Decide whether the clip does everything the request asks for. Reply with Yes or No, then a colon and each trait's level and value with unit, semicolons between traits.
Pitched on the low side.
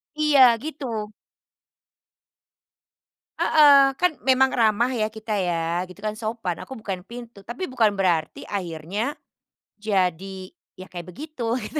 No: high, 215 Hz